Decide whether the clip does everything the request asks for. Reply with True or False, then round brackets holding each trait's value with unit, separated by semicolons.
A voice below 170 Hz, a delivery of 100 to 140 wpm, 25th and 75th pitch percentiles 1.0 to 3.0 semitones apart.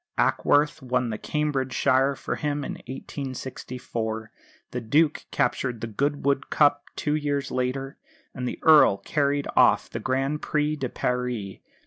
True (135 Hz; 135 wpm; 2.6 semitones)